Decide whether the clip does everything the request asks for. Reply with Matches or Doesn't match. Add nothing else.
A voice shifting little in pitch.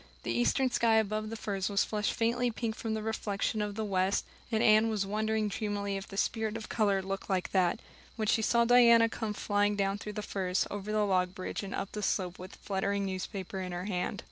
Matches